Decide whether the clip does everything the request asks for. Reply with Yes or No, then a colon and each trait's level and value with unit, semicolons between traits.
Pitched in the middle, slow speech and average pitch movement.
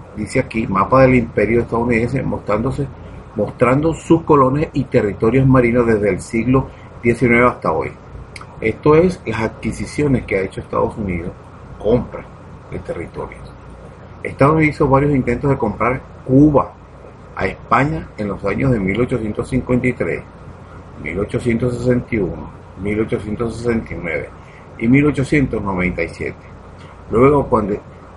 No: low, 120 Hz; slow, 110 wpm; average, 3.8 semitones